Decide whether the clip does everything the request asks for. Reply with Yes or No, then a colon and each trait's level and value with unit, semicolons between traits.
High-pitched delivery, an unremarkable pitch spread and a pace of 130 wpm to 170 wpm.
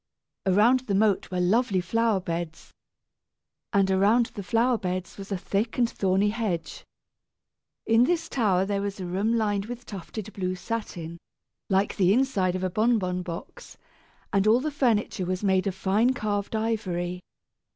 Yes: high, 200 Hz; average, 3.5 semitones; average, 160 wpm